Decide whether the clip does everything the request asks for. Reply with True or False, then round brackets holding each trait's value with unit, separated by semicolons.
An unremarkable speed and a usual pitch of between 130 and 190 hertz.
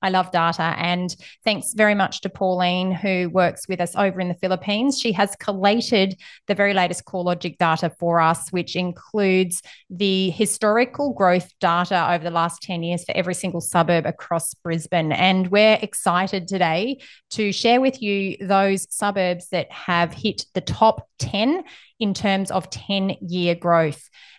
True (160 wpm; 185 Hz)